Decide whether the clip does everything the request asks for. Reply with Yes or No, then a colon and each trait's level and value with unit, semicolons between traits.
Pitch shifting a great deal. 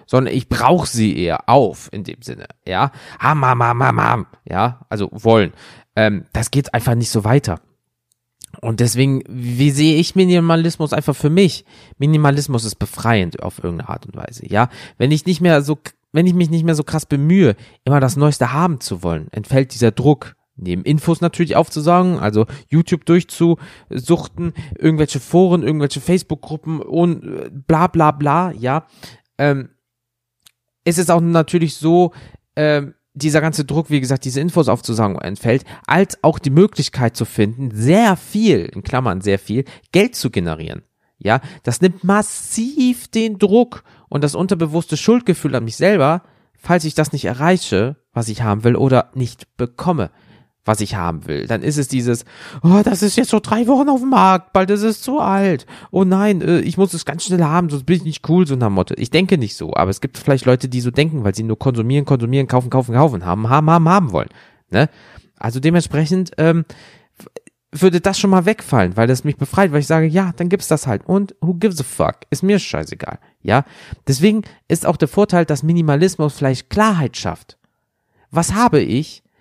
Yes: wide, 6.1 semitones